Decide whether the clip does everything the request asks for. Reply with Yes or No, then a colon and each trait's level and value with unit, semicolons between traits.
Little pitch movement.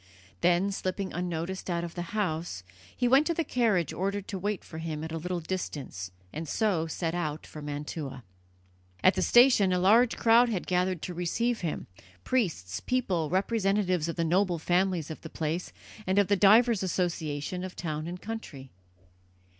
No: average, 3.7 semitones